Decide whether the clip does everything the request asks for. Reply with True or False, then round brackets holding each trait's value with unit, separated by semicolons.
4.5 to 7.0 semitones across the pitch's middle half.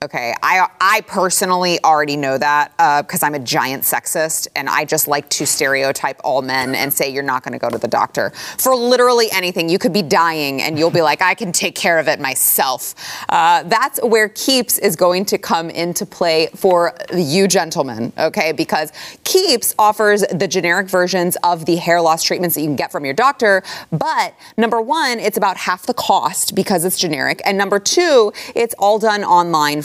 True (5.0 semitones)